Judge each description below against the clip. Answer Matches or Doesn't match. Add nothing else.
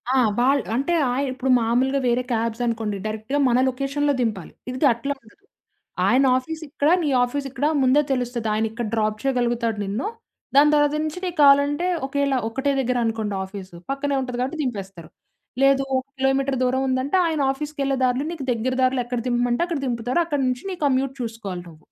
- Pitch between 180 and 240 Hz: Doesn't match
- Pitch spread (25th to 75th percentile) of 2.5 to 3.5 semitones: Matches